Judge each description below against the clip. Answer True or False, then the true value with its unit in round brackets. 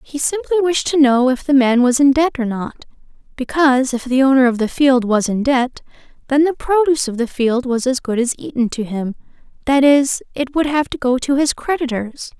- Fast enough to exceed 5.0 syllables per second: True (5.4 syllables/s)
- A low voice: False (265 Hz)